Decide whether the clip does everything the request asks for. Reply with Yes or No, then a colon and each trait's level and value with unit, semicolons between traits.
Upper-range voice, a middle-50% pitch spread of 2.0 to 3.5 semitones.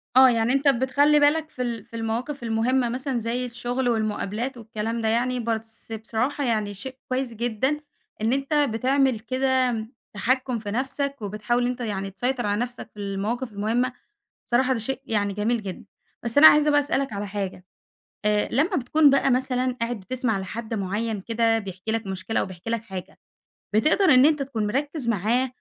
Yes: high, 235 Hz; average, 3.2 semitones